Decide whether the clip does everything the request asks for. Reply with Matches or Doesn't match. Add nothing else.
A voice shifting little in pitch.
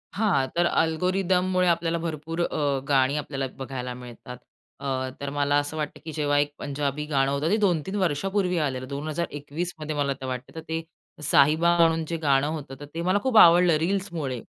Doesn't match